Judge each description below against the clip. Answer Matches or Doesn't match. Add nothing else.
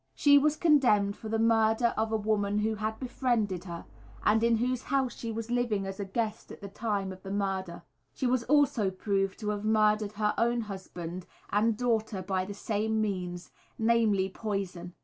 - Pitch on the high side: Matches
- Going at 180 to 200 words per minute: Matches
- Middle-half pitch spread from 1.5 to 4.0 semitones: Matches